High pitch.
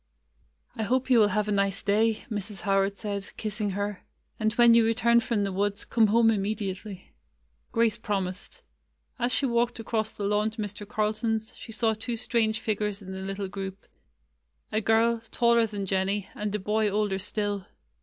Yes: high, 210 Hz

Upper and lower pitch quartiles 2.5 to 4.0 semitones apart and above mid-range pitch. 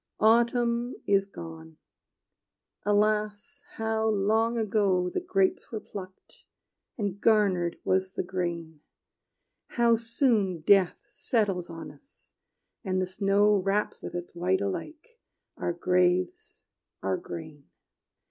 Yes: average, 3.7 semitones; high, 200 Hz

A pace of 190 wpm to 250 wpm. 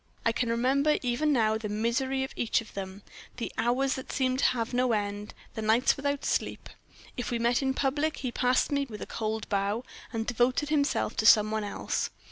Yes: fast, 205 wpm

